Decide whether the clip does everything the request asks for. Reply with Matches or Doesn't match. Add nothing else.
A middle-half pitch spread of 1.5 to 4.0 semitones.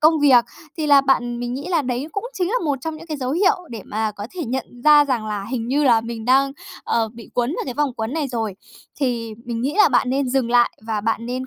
Matches